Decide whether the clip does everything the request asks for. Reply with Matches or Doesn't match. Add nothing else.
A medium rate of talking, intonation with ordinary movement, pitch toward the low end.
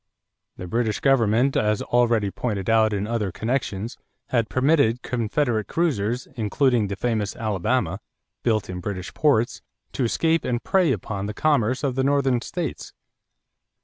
Matches